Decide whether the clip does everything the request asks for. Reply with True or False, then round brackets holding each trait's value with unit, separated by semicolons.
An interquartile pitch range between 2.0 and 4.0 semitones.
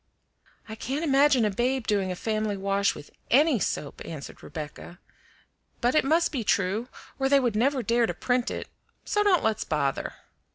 False (5.3 semitones)